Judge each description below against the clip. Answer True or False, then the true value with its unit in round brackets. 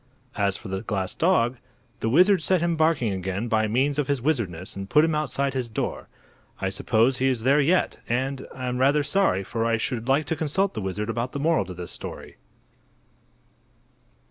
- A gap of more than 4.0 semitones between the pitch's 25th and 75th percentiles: True (5.4 semitones)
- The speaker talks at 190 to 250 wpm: True (195 wpm)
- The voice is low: True (130 Hz)